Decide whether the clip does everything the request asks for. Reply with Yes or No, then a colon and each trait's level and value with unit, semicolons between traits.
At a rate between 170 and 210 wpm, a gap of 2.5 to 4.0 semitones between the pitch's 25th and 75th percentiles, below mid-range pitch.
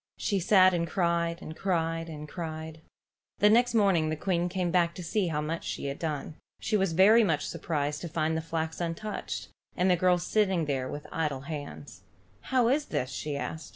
No: average, 195 wpm; average, 3.1 semitones; medium, 165 Hz